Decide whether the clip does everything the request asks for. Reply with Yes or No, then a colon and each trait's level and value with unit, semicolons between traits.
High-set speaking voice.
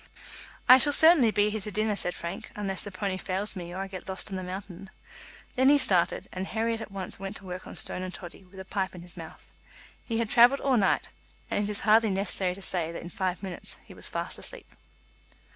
Yes: high, 195 Hz